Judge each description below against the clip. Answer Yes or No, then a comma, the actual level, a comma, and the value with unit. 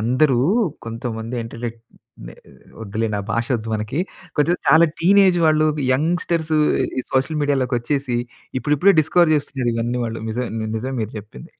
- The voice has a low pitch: Yes, low, 125 Hz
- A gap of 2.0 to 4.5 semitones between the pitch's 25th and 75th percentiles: No, average, 5.3 semitones